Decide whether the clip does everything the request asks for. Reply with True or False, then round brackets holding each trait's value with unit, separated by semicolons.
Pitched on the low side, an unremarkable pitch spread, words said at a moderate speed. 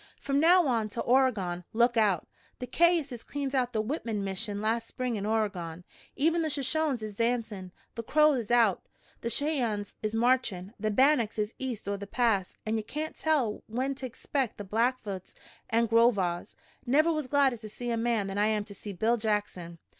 False (230 Hz; 4.0 semitones; 190 wpm)